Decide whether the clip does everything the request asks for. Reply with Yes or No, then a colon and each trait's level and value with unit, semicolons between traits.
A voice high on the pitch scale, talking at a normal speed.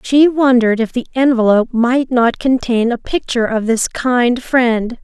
Yes: high, 240 Hz; average, 165 wpm